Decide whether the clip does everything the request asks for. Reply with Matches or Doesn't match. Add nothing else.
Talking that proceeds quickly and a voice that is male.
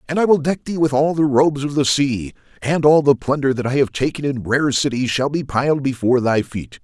Matches